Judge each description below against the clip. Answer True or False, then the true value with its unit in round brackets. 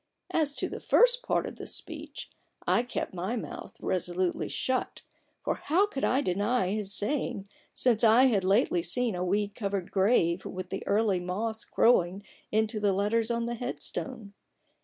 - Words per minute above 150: True (170 wpm)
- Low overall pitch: False (215 Hz)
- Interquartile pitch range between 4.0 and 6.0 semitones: True (4.4 semitones)